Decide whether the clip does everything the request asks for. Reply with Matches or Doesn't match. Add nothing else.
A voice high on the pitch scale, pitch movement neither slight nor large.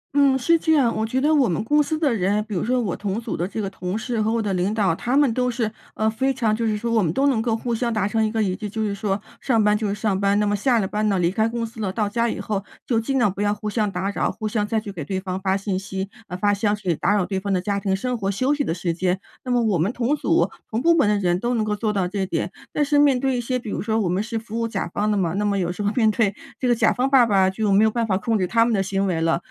Matches